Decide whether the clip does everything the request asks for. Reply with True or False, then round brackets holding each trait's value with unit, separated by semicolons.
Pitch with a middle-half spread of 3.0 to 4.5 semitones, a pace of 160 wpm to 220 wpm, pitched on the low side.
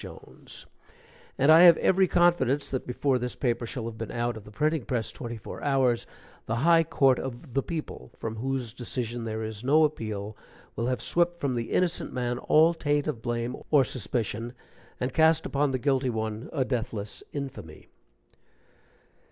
True (4.0 semitones; 175 wpm; 125 Hz)